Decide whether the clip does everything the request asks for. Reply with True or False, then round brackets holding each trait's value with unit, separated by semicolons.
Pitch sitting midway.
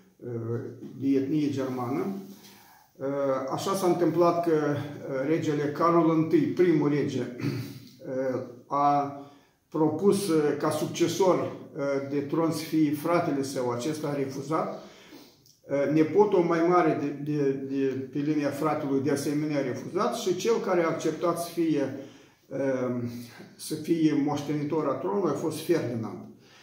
True (150 Hz)